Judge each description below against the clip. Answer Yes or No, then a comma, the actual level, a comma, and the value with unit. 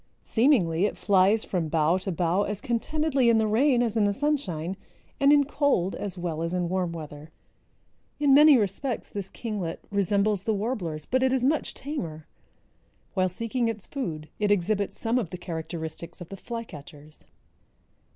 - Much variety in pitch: Yes, wide, 6.0 semitones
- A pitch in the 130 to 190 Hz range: No, high, 200 Hz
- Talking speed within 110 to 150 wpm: No, average, 170 wpm